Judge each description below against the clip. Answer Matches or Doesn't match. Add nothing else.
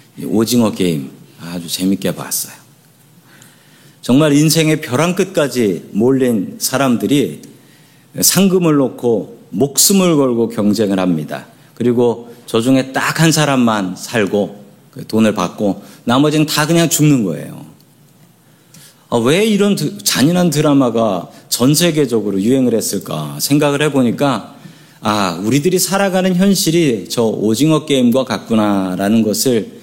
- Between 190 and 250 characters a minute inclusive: Doesn't match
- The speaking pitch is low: Matches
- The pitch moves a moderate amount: Doesn't match